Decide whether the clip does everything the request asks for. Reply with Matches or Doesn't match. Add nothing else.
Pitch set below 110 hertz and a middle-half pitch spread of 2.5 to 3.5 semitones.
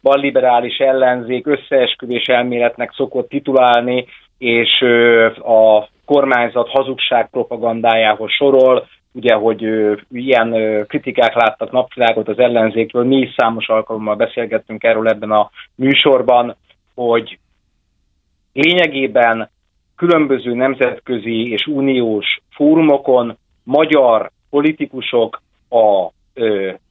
Doesn't match